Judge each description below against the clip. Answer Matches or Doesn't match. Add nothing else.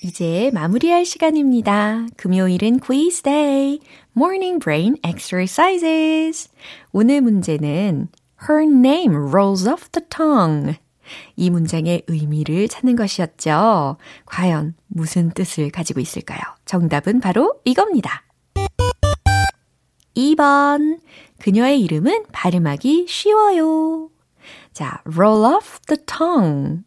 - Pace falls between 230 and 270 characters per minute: Doesn't match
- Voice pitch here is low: Doesn't match